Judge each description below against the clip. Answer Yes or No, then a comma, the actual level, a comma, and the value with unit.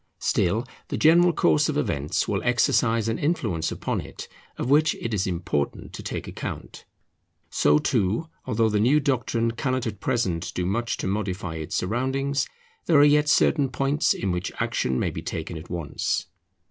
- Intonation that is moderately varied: No, wide, 7.4 semitones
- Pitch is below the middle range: Yes, low, 115 Hz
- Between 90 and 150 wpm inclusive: No, average, 170 wpm